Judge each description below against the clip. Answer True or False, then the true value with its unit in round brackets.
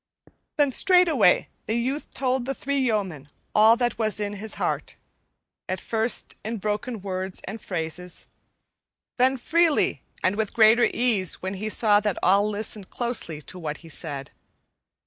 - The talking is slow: False (150 wpm)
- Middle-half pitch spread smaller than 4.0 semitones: False (4.5 semitones)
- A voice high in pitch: True (215 Hz)